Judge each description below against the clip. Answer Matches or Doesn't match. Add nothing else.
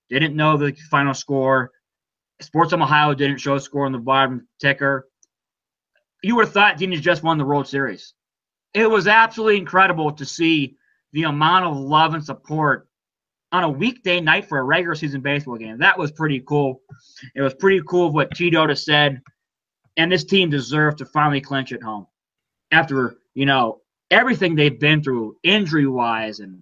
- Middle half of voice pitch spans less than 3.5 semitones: Doesn't match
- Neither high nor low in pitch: Matches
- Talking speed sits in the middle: Matches